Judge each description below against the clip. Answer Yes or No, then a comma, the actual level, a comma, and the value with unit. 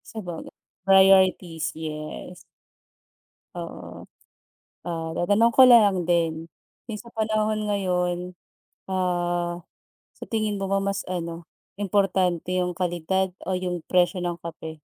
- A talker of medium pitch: Yes, medium, 180 Hz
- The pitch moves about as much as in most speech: No, narrow, 2.3 semitones